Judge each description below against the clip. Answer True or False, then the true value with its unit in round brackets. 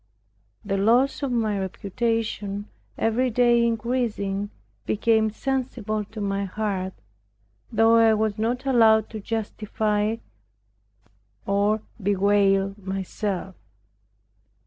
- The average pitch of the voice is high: True (215 Hz)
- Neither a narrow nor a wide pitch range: False (2.3 semitones)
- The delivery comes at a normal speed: False (95 wpm)